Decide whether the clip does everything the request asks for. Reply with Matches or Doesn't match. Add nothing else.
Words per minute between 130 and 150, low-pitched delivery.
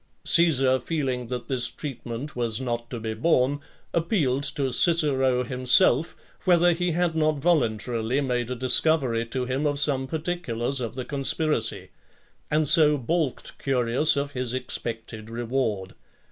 Matches